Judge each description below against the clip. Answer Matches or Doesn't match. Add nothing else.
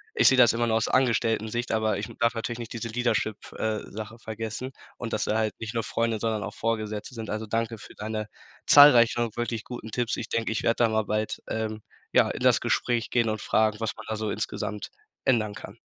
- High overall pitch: Doesn't match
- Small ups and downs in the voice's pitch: Matches